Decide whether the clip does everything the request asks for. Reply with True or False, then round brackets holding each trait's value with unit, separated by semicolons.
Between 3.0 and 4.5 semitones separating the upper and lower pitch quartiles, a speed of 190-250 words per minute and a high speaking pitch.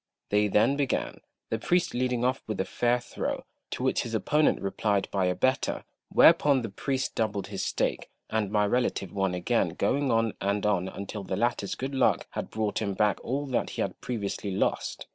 False (4.0 semitones; 195 wpm; 110 Hz)